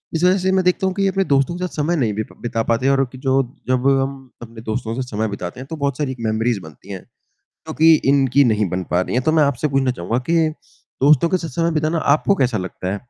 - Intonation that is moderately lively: No, wide, 5.8 semitones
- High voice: No, low, 135 Hz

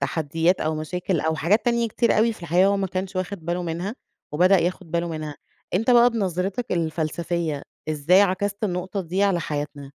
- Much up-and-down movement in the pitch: No, average, 3.7 semitones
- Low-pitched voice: No, medium, 180 Hz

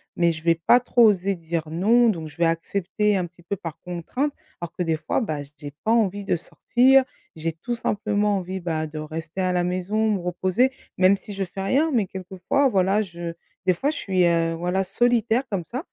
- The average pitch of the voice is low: No, medium, 185 Hz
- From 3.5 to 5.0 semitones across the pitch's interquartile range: Yes, average, 4.1 semitones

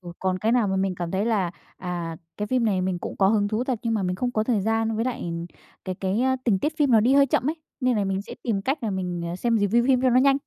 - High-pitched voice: Yes, high, 215 Hz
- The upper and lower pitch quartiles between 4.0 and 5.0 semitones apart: Yes, average, 4.6 semitones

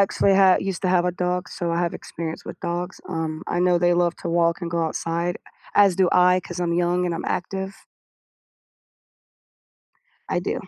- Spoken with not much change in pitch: Yes, narrow, 1.2 semitones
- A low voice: No, medium, 175 Hz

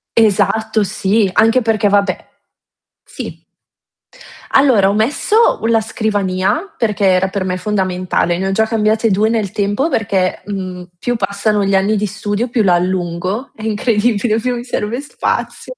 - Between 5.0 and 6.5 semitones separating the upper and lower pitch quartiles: No, average, 2.7 semitones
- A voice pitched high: Yes, high, 210 Hz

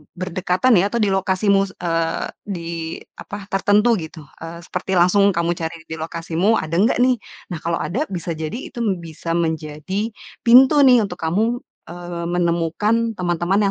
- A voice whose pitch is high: No, medium, 180 Hz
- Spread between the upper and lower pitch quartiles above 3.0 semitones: Yes, average, 3.6 semitones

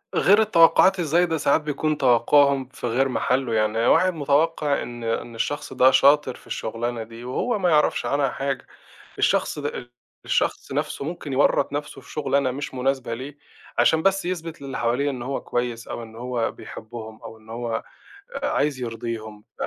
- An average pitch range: Yes, average, 4.0 semitones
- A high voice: No, low, 135 Hz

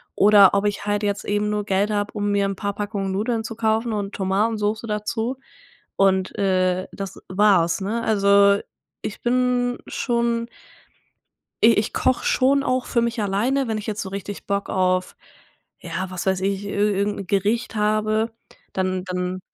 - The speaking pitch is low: No, high, 205 Hz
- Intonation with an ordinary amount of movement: No, narrow, 2.3 semitones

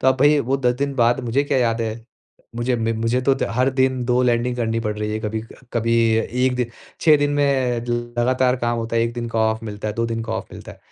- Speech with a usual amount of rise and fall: No, narrow, 2.1 semitones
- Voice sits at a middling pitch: No, low, 120 Hz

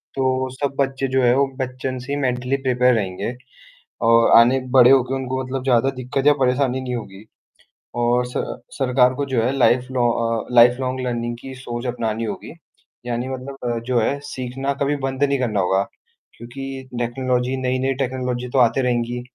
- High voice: No, low, 125 Hz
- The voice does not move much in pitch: Yes, narrow, 1.7 semitones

